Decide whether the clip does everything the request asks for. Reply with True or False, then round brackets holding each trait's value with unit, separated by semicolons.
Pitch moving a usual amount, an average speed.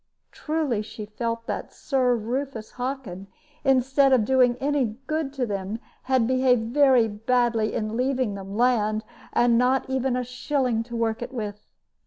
True (3.0 semitones; 155 wpm)